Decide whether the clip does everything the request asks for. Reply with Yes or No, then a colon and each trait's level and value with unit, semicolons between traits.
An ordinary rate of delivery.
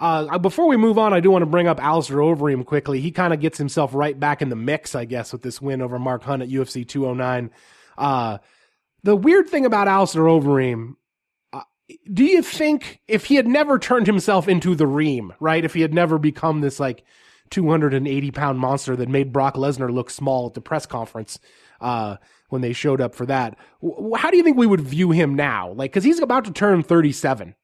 No: fast, 215 wpm